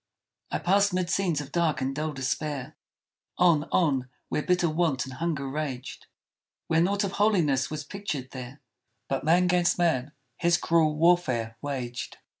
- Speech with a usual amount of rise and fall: Yes, average, 4.5 semitones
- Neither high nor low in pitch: Yes, medium, 155 Hz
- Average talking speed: Yes, average, 155 wpm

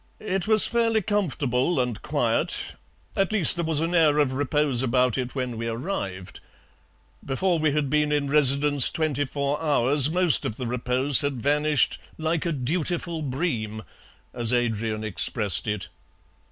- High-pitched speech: No, medium, 145 Hz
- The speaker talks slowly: No, average, 155 wpm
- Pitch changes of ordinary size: Yes, average, 4.5 semitones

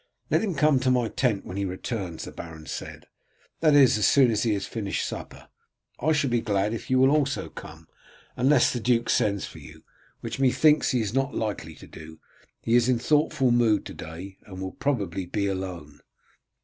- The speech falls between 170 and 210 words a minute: Yes, average, 200 wpm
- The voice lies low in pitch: Yes, low, 115 Hz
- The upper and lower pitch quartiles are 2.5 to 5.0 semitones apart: No, wide, 5.4 semitones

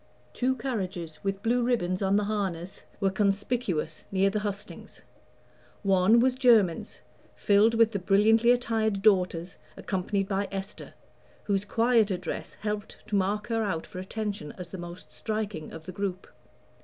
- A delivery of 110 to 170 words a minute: Yes, average, 150 wpm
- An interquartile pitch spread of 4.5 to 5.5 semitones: No, average, 2.8 semitones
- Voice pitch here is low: No, high, 200 Hz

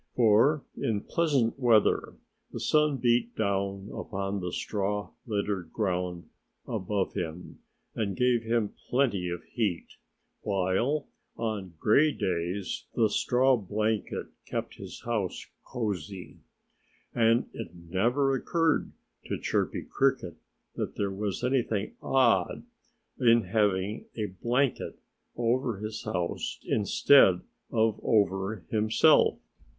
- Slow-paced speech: Yes, slow, 110 wpm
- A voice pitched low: Yes, low, 105 Hz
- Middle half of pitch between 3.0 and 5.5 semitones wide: Yes, average, 3.7 semitones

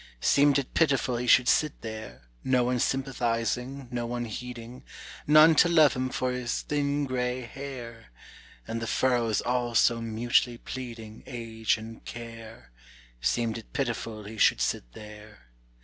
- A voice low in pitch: Yes, low, 120 Hz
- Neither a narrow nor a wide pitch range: No, narrow, 2.3 semitones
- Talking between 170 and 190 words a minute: No, average, 150 wpm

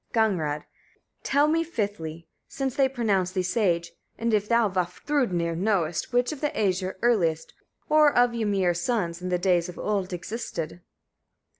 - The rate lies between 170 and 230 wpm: No, average, 150 wpm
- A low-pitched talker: No, high, 195 Hz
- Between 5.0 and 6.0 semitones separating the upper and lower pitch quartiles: Yes, wide, 5.4 semitones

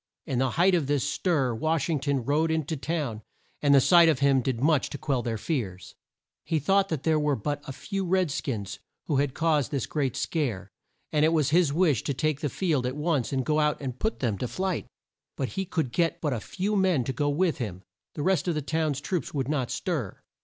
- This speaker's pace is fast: Yes, fast, 235 wpm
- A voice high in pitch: No, medium, 145 Hz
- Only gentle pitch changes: No, average, 3.8 semitones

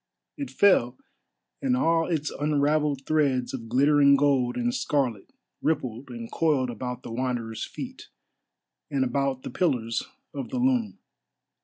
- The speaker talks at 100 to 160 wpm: Yes, slow, 135 wpm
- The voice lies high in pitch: No, medium, 140 Hz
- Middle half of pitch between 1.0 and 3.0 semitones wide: No, average, 3.8 semitones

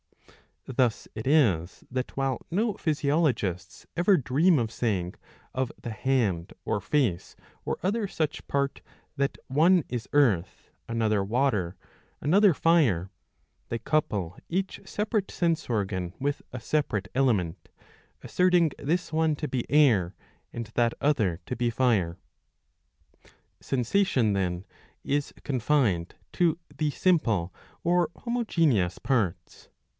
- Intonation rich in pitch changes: Yes, wide, 7.6 semitones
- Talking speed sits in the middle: No, slow, 120 wpm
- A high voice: No, low, 130 Hz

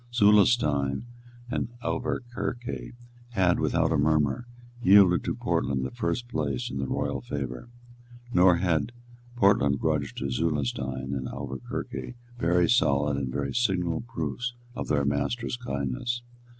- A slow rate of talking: Yes, slow, 125 wpm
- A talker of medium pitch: No, very low, 80 Hz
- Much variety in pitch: Yes, wide, 8.9 semitones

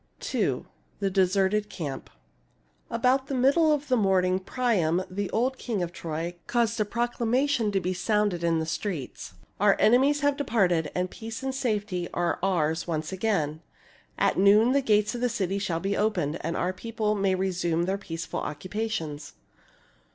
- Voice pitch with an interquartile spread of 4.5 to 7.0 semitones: Yes, average, 4.9 semitones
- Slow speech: No, average, 170 wpm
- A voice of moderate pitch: No, high, 200 Hz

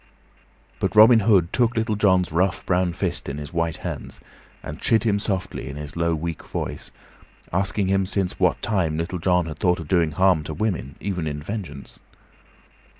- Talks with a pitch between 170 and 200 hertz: No, very low, 90 Hz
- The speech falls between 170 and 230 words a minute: Yes, average, 180 wpm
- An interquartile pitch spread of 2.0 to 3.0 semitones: No, average, 3.7 semitones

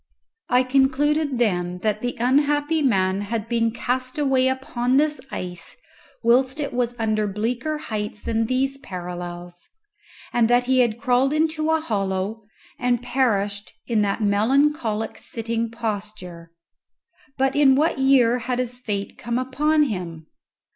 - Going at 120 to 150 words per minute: Yes, average, 140 wpm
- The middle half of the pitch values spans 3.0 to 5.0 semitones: Yes, average, 4.1 semitones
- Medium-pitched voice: No, high, 240 Hz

